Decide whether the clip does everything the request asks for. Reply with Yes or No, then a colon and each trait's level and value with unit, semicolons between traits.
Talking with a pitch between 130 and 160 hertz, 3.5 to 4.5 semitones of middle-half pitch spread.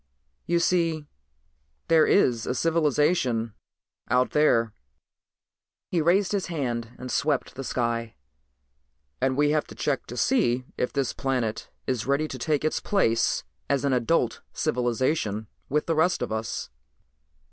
No: low, 135 Hz; average, 5.0 semitones